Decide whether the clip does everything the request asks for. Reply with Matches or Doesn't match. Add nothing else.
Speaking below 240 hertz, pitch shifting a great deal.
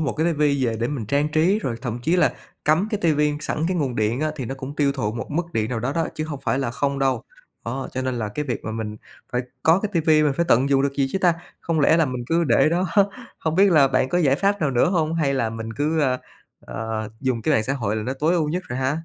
Doesn't match